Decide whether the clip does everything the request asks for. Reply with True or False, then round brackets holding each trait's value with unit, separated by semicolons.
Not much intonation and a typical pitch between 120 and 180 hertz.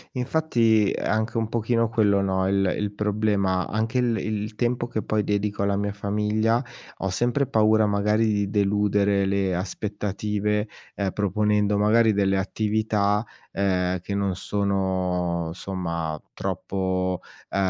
False (1.9 semitones; 105 Hz)